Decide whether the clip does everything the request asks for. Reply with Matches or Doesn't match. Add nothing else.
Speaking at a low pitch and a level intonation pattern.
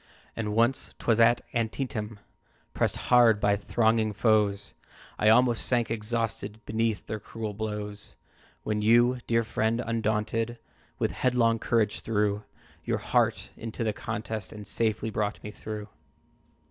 Matches